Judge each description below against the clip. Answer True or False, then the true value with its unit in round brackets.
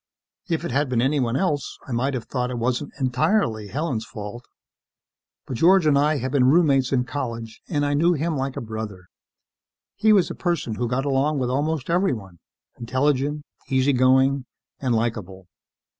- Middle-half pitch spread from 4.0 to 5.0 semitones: False (3.6 semitones)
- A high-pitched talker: False (130 Hz)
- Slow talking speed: False (175 wpm)